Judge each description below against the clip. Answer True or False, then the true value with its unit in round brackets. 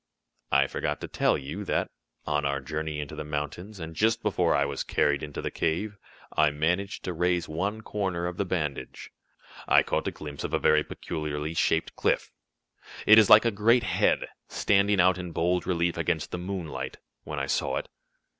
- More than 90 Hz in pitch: False (85 Hz)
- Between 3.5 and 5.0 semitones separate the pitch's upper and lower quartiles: True (4.6 semitones)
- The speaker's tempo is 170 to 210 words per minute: True (190 wpm)